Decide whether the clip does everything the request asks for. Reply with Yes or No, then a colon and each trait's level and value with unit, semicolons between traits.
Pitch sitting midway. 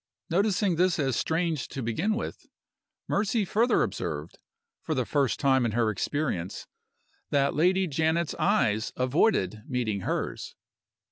Yes: medium, 150 Hz